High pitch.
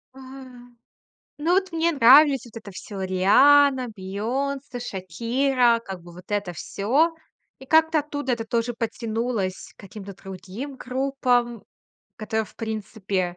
Yes: high, 235 Hz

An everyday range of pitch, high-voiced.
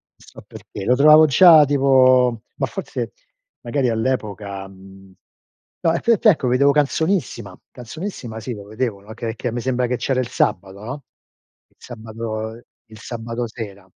No: average, 3.8 semitones; low, 120 Hz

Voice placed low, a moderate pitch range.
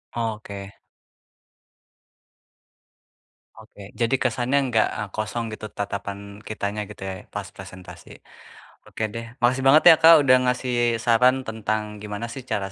Yes: low, 110 Hz; average, 3.0 semitones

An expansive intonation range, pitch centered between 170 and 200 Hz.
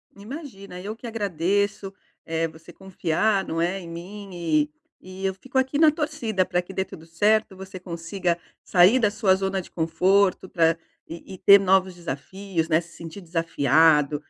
No: average, 3.3 semitones; medium, 185 Hz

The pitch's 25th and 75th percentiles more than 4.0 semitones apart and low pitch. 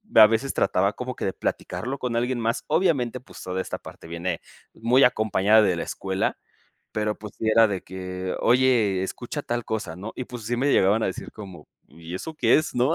Yes: average, 4.7 semitones; low, 110 Hz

